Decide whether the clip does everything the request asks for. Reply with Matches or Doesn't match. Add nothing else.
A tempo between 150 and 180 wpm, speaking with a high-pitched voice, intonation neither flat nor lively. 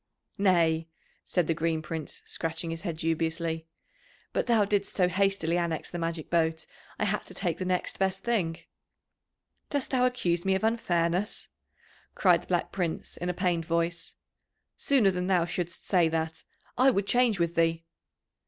Doesn't match